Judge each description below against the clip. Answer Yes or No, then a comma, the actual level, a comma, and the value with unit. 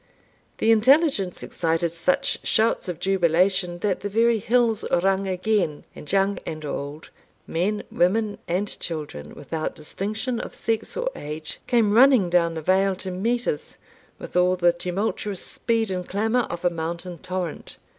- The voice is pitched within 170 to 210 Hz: Yes, medium, 185 Hz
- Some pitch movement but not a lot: Yes, average, 4.1 semitones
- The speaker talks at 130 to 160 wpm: Yes, average, 155 wpm